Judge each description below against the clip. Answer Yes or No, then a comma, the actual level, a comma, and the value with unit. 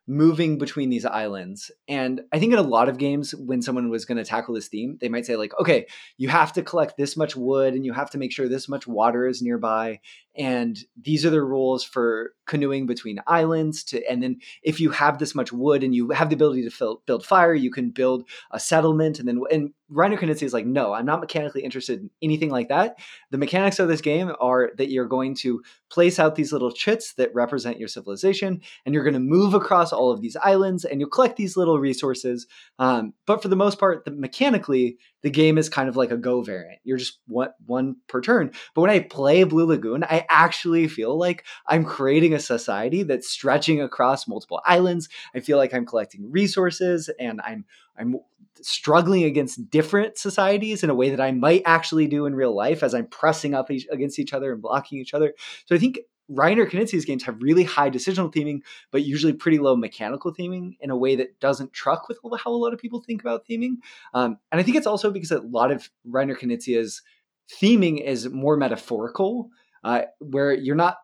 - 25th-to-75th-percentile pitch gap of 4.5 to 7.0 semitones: Yes, average, 5.3 semitones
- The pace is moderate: No, fast, 220 wpm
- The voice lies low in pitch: No, medium, 145 Hz